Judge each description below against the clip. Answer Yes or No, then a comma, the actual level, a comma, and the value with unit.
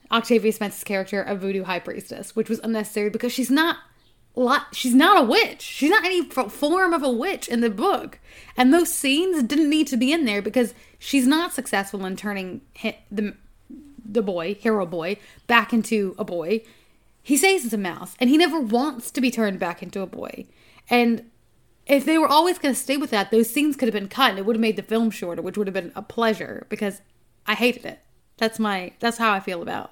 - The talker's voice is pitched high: Yes, high, 230 Hz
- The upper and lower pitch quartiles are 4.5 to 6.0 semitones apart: Yes, average, 5.1 semitones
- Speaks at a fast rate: Yes, fast, 220 wpm